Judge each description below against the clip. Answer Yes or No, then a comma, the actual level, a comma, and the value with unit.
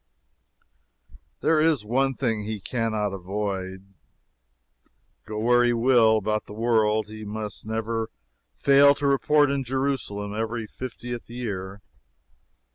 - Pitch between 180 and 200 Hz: No, low, 110 Hz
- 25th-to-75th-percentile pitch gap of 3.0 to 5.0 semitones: Yes, average, 3.3 semitones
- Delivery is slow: Yes, slow, 120 wpm